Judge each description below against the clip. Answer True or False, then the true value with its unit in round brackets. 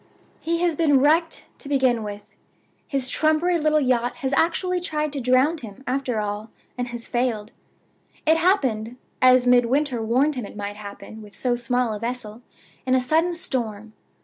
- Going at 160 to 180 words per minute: True (170 wpm)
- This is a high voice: True (255 Hz)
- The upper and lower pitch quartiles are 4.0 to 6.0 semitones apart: True (4.8 semitones)